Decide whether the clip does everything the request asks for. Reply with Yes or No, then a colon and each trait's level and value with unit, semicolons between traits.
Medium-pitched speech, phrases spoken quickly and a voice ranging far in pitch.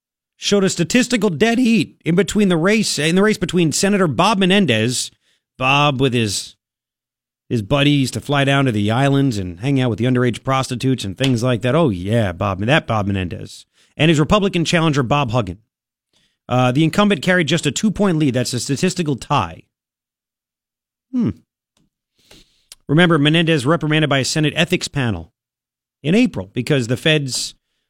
No: medium, 145 Hz; average, 165 wpm; wide, 5.9 semitones